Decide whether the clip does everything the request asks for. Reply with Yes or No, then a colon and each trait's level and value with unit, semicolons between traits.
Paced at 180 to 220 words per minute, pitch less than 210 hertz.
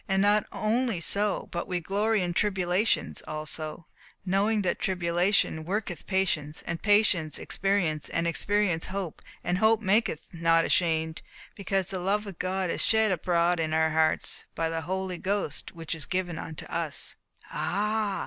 No: average, 155 wpm; medium, 185 Hz